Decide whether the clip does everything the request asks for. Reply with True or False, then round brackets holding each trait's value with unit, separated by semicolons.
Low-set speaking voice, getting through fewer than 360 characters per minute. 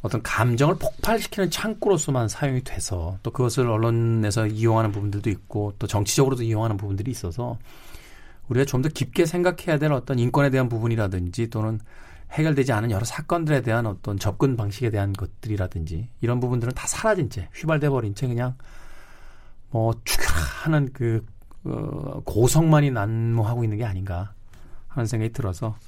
False (115 Hz; 370 characters per minute)